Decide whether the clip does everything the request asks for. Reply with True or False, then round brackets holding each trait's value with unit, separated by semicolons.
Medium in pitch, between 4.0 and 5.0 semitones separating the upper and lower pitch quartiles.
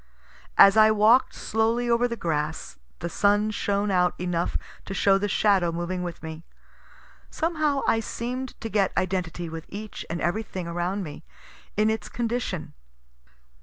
False (200 Hz; 4.3 semitones)